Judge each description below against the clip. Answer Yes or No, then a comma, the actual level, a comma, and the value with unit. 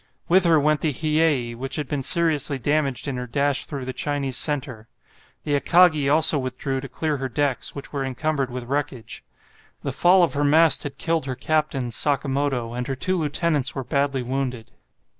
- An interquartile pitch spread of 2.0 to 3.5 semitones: Yes, average, 2.8 semitones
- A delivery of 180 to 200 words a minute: Yes, average, 185 wpm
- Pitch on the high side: No, medium, 140 Hz